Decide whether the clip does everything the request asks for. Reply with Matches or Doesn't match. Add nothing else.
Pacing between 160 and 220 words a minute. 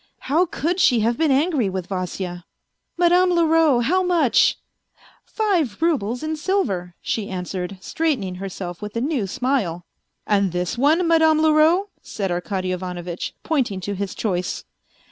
Matches